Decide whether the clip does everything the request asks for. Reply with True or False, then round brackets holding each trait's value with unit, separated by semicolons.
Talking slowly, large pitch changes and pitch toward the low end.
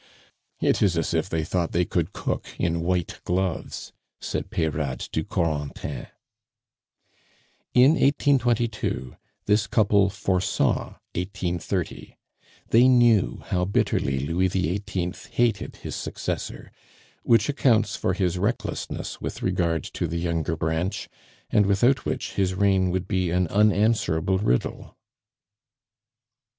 False (115 wpm; 3.8 semitones; 95 Hz)